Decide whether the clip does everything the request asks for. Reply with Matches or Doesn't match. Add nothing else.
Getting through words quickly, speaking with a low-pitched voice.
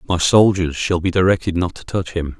Matches